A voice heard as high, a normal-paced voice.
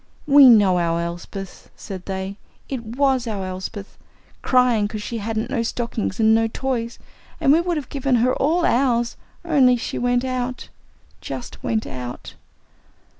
Yes: high, 235 Hz; average, 155 wpm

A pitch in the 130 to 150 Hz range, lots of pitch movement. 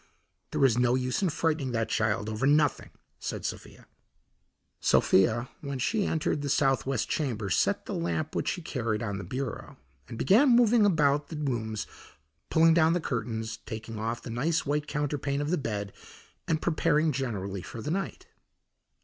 Yes: low, 135 Hz; wide, 5.7 semitones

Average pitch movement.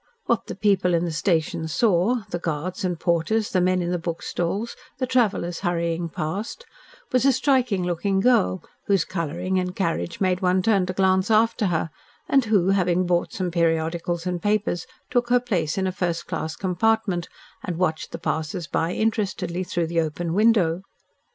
Yes: average, 3.4 semitones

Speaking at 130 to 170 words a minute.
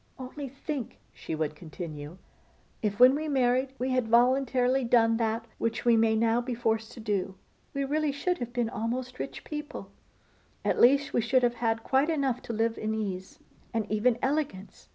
No: average, 180 wpm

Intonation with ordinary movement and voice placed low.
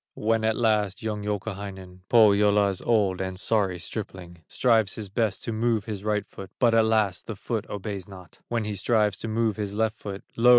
No: narrow, 2.3 semitones; low, 105 Hz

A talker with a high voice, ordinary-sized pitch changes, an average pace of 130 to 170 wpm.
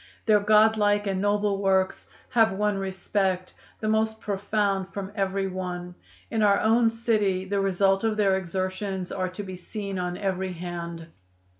No: high, 195 Hz; narrow, 1.9 semitones; average, 160 wpm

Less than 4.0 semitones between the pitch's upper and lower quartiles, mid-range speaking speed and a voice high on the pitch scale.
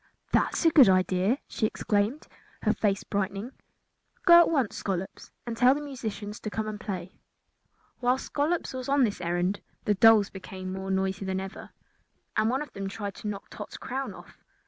No: average, 4.8 semitones; average, 185 wpm; high, 210 Hz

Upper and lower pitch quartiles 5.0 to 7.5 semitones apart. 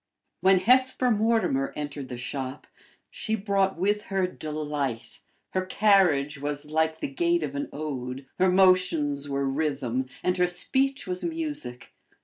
Yes: wide, 5.6 semitones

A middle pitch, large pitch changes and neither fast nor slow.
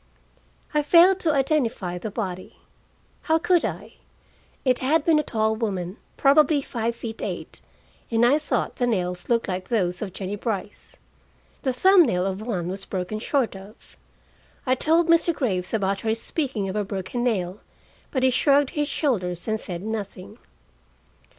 No: high, 225 Hz; wide, 6.6 semitones; average, 165 wpm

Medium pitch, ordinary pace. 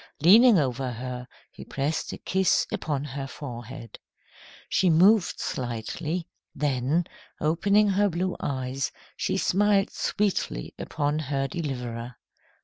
No: medium, 150 Hz; slow, 115 wpm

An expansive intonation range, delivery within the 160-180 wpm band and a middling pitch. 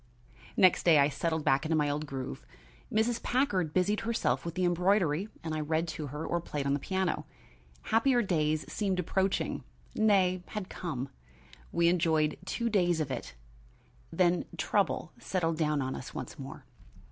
No: average, 3.9 semitones; average, 165 wpm; medium, 170 Hz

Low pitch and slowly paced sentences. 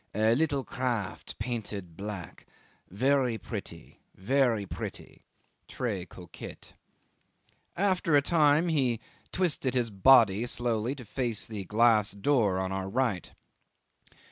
Yes: low, 115 Hz; slow, 115 wpm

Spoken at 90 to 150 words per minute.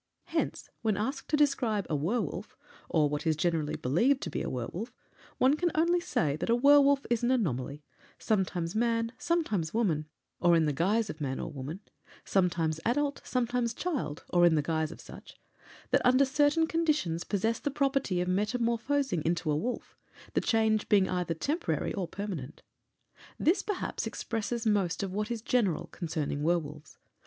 No: average, 170 wpm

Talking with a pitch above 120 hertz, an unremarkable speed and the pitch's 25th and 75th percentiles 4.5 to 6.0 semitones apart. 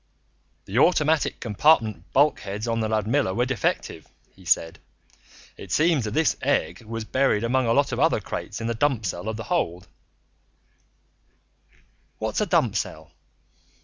No: low, 115 Hz; average, 155 wpm; average, 5.1 semitones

